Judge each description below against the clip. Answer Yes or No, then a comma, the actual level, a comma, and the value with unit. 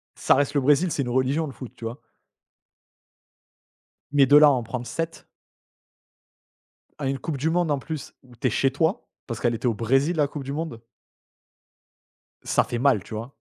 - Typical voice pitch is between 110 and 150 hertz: Yes, low, 135 Hz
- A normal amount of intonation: Yes, average, 3.4 semitones